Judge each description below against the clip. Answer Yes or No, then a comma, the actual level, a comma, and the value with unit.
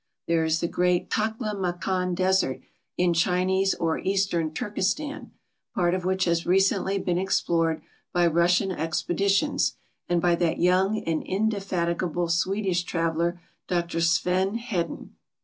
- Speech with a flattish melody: Yes, narrow, 2.2 semitones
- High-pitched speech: No, medium, 180 Hz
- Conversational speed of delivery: No, slow, 120 wpm